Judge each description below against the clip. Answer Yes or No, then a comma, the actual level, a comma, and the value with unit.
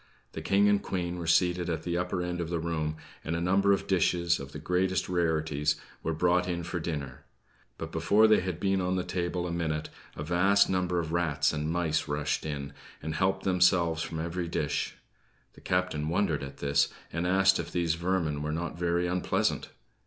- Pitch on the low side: Yes, very low, 85 Hz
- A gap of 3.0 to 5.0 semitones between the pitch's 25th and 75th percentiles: No, narrow, 2.4 semitones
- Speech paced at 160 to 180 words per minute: No, average, 195 wpm